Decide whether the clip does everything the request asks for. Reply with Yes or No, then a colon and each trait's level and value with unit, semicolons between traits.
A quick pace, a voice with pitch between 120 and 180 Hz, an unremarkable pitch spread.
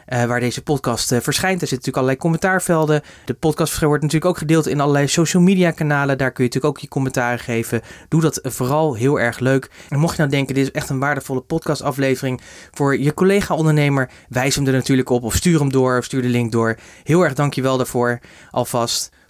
Yes: fast, 215 wpm; medium, 140 Hz; average, 3.4 semitones